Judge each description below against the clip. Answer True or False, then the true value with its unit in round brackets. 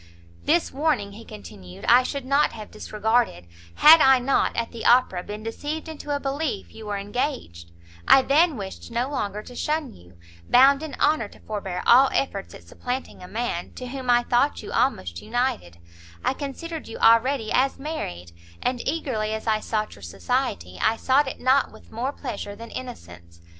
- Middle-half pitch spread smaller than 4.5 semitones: False (5.2 semitones)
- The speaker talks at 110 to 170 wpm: False (180 wpm)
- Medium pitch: False (240 Hz)